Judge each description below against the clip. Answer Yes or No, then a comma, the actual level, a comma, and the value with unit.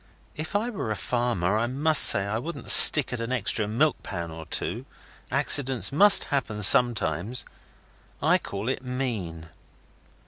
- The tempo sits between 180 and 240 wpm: No, average, 150 wpm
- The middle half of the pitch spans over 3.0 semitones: Yes, average, 5.2 semitones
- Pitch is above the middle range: No, low, 120 Hz